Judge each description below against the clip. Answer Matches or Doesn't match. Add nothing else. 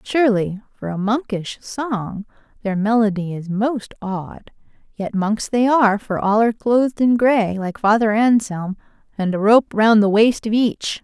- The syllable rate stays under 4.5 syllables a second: Matches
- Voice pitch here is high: Matches